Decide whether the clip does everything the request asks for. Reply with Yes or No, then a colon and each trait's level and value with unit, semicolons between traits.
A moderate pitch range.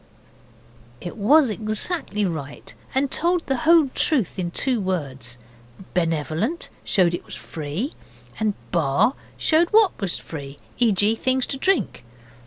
No: wide, 8.3 semitones